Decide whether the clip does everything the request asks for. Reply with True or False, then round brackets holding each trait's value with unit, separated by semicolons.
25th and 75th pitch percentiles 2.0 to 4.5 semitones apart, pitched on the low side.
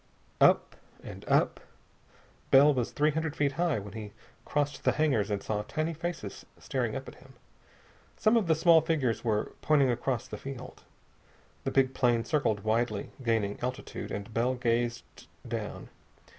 False (5.1 semitones; 130 Hz)